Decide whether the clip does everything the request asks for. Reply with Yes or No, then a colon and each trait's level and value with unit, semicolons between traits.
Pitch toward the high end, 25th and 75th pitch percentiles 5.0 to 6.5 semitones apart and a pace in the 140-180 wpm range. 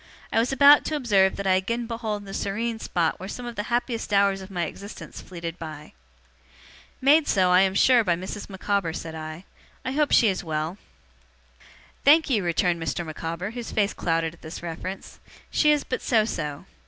No: high, 195 Hz; average, 5.3 semitones; average, 190 wpm